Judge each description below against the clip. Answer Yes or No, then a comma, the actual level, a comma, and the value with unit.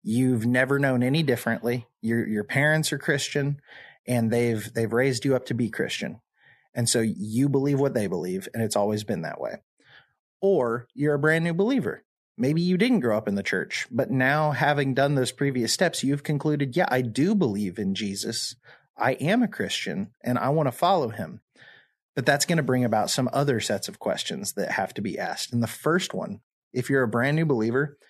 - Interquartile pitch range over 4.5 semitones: No, average, 4.1 semitones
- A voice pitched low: Yes, low, 130 Hz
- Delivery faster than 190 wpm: Yes, fast, 205 wpm